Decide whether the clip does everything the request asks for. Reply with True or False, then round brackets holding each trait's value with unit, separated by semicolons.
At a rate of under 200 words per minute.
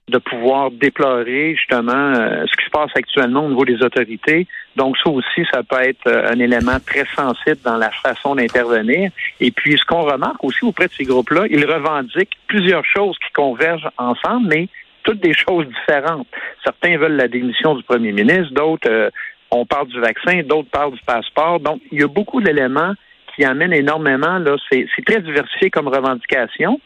True (190 wpm)